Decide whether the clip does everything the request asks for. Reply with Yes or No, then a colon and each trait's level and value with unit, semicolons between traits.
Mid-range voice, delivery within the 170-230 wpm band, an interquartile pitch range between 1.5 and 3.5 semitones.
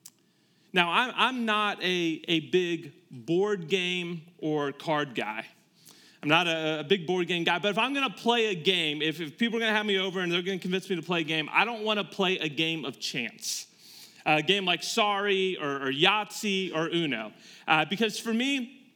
No: medium, 180 Hz; fast, 205 wpm; average, 4.2 semitones